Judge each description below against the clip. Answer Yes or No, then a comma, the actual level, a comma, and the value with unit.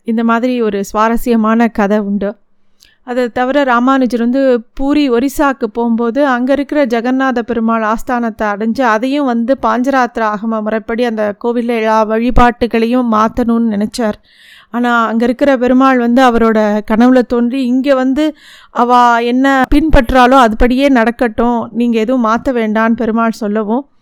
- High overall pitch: Yes, high, 240 Hz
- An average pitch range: No, narrow, 2.2 semitones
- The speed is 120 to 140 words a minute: Yes, average, 125 wpm